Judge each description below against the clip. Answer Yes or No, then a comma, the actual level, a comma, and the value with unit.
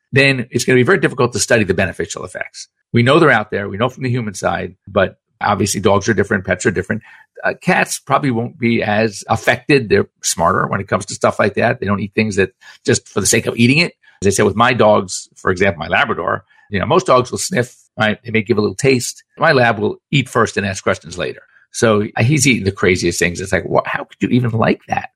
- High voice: No, low, 115 Hz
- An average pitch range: Yes, average, 3.2 semitones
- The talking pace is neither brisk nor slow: No, fast, 255 wpm